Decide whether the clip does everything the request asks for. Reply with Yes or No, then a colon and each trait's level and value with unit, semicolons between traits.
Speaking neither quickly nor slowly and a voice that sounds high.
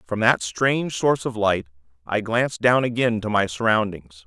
No: average, 185 wpm; low, 110 Hz